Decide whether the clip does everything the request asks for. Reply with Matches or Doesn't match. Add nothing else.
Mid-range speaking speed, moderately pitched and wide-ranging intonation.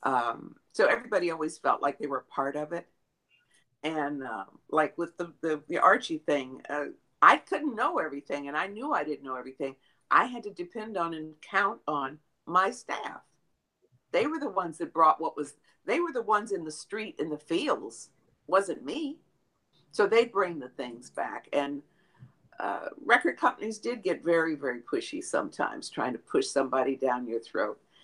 Matches